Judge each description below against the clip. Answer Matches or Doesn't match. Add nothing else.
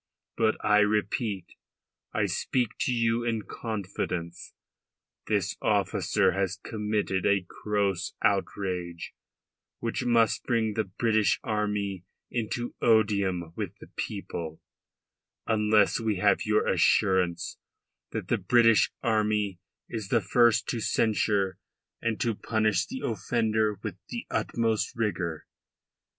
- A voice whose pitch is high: Doesn't match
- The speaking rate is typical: Doesn't match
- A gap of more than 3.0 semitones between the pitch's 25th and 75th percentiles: Doesn't match